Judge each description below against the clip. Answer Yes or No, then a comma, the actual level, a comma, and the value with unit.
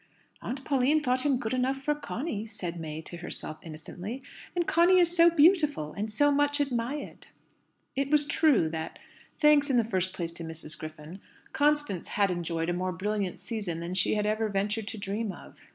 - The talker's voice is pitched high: Yes, high, 220 Hz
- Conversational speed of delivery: Yes, average, 185 wpm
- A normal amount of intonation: No, wide, 8.4 semitones